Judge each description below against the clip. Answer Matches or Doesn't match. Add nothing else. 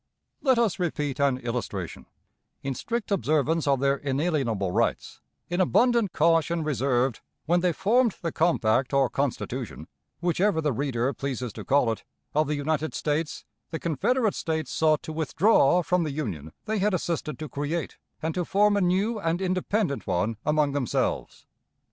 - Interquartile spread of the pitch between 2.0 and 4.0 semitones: Doesn't match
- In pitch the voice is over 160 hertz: Doesn't match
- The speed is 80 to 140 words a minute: Doesn't match